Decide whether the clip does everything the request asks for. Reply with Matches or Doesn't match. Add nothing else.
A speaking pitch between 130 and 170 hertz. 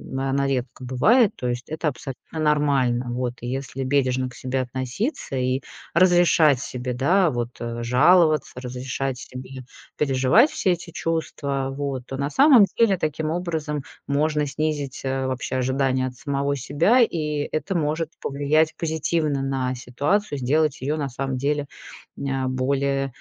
Matches